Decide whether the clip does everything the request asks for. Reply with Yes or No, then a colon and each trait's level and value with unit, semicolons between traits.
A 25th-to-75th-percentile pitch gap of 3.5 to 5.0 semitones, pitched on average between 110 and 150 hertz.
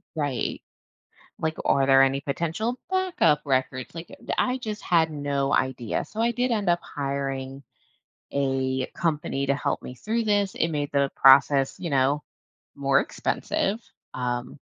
Yes: average, 4.5 semitones; medium, 140 Hz